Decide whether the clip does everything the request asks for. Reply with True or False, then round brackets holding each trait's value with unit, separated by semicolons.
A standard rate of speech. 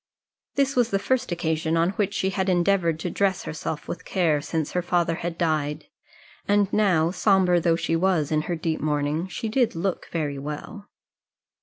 True (180 wpm)